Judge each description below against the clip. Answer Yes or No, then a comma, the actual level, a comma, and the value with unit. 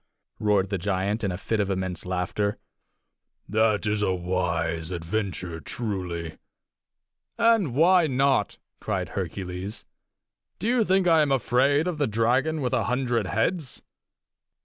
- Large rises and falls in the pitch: Yes, wide, 6.7 semitones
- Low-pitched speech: Yes, low, 105 Hz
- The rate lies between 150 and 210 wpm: No, slow, 135 wpm